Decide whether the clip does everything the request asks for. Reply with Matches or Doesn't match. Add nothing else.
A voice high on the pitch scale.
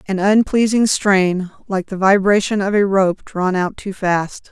Matches